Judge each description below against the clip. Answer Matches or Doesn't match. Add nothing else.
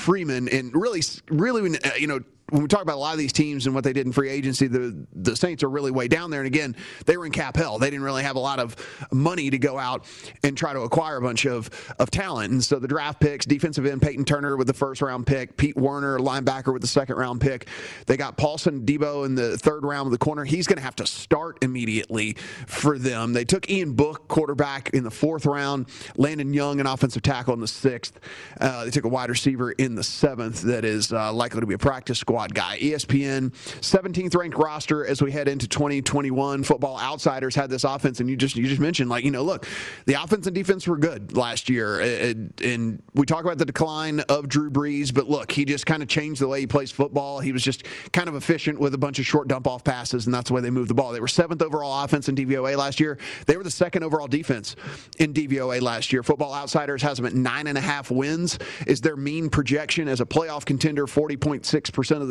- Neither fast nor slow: Doesn't match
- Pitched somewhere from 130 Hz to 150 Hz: Matches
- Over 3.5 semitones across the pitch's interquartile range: Doesn't match